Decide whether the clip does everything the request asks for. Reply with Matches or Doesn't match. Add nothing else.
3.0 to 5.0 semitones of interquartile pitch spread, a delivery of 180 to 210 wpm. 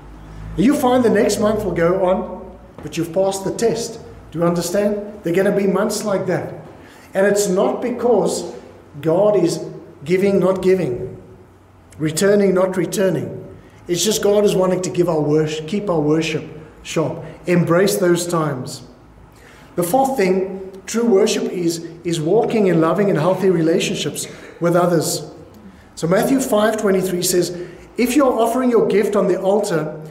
Doesn't match